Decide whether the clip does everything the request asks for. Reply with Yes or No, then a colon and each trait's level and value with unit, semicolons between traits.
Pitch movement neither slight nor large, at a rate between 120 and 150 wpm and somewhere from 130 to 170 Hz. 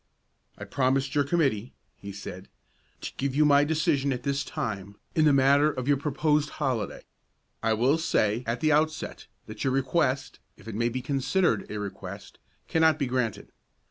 No: average, 4.4 semitones; average, 175 wpm; low, 135 Hz